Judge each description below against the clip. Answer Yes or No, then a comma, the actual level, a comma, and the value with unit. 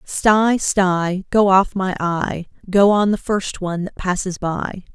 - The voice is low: No, high, 190 Hz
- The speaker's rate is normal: Yes, average, 170 wpm